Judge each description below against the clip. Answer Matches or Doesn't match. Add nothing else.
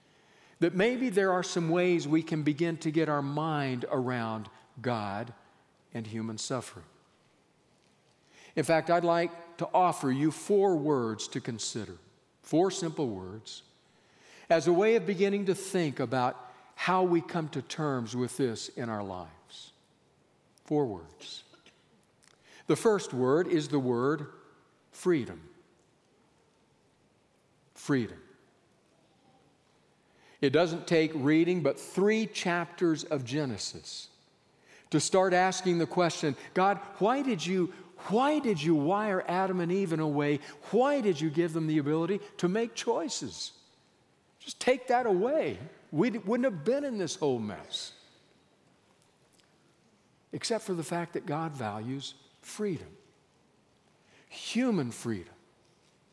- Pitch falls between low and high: Matches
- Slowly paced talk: Matches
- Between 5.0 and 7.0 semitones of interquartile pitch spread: Matches